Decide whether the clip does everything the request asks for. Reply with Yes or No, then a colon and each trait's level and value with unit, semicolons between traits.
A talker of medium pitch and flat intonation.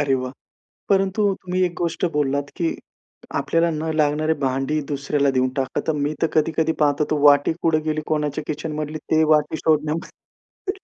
Yes: medium, 155 Hz; narrow, 2.0 semitones